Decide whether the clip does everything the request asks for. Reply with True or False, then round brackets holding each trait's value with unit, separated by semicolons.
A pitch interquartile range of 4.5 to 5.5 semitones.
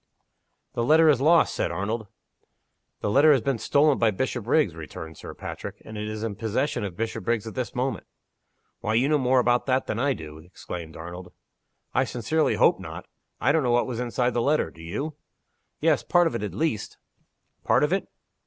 True (5.2 semitones)